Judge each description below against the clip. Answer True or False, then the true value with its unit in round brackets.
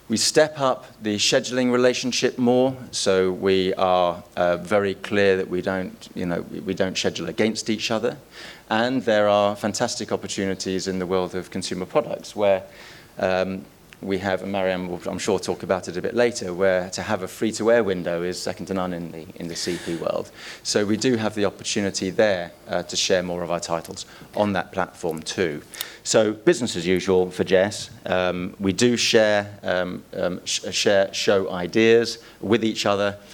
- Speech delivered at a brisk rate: False (185 wpm)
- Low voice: True (100 Hz)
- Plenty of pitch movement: False (3.4 semitones)